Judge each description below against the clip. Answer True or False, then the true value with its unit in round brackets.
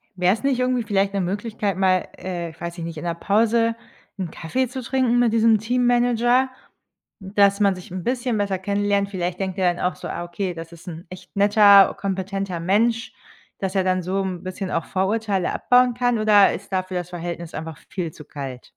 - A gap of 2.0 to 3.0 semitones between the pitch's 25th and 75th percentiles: False (3.8 semitones)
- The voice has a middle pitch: False (195 Hz)